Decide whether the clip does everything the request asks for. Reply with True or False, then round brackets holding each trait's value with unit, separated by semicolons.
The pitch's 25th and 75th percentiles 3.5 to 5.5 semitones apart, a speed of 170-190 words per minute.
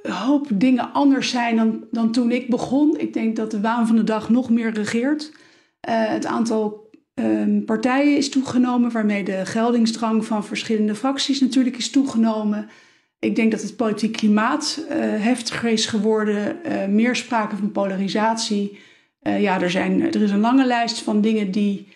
False (3.0 semitones; 175 wpm)